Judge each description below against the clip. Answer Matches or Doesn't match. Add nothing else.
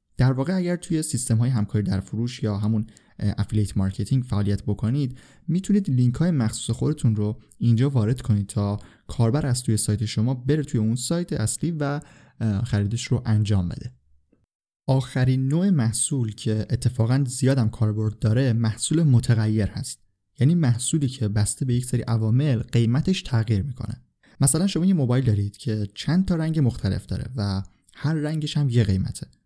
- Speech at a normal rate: Doesn't match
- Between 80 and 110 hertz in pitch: Doesn't match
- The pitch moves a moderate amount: Matches